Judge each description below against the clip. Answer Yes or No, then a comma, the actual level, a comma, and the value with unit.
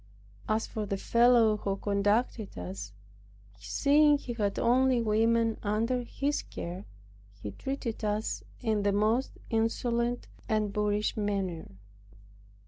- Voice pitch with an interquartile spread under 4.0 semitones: Yes, average, 2.8 semitones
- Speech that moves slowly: Yes, slow, 120 wpm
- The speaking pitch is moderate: No, high, 220 Hz